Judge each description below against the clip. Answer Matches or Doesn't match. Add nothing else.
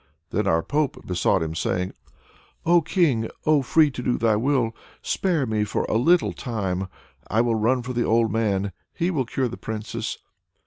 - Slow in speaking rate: Doesn't match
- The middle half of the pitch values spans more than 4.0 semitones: Matches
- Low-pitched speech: Matches